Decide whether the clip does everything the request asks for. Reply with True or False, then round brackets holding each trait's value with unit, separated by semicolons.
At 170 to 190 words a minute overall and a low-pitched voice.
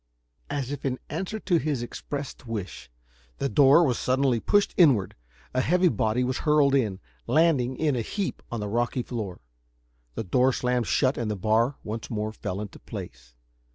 True (175 wpm; 125 Hz)